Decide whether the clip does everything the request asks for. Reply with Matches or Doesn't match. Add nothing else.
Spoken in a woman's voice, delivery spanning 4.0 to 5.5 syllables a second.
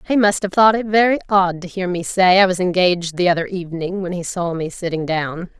Doesn't match